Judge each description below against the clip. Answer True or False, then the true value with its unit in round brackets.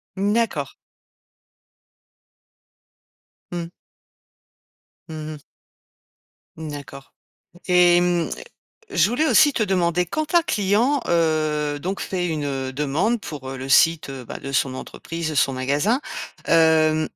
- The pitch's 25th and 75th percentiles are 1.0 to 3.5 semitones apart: False (4.6 semitones)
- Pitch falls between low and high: True (165 Hz)